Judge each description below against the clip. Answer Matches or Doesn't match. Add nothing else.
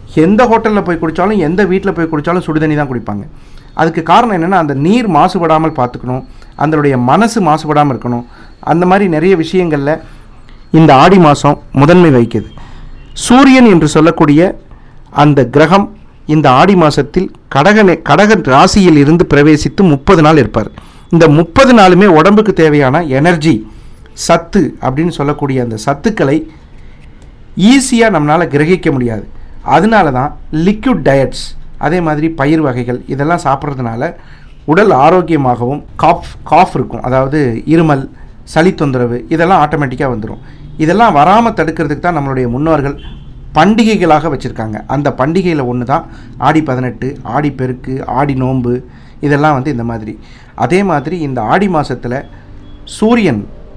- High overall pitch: Doesn't match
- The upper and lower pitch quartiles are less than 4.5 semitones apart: Doesn't match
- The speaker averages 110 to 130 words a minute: Matches